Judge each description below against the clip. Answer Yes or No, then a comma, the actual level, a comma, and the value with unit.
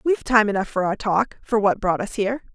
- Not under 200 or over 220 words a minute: No, fast, 260 wpm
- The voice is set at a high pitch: Yes, high, 215 Hz